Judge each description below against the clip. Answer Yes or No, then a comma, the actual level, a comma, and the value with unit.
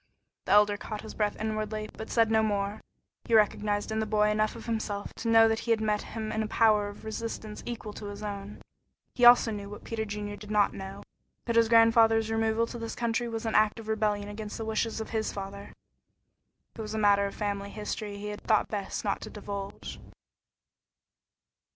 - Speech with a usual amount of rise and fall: No, narrow, 1.3 semitones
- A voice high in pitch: Yes, high, 215 Hz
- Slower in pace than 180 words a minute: No, fast, 205 wpm